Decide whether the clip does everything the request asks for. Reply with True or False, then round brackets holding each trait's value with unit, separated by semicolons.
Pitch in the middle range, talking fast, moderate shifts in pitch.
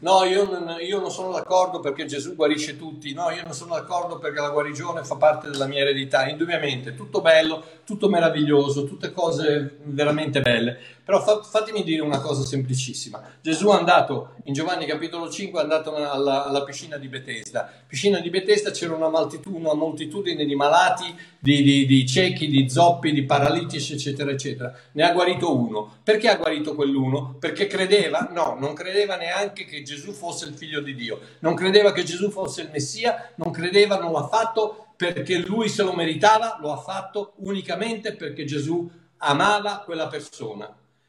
True (160 Hz; 175 wpm; 4.5 semitones)